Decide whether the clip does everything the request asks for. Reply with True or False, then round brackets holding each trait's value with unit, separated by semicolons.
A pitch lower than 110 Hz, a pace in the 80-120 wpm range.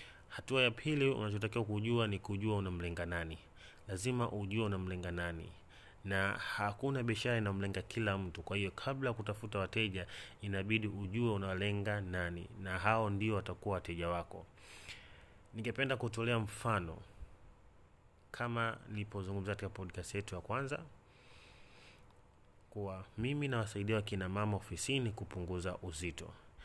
True (100 Hz; 115 wpm)